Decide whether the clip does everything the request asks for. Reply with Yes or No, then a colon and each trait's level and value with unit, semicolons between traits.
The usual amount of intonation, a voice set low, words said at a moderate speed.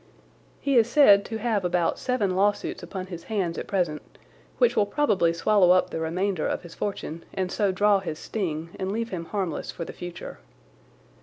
No: average, 3.4 semitones; high, 190 Hz; average, 185 wpm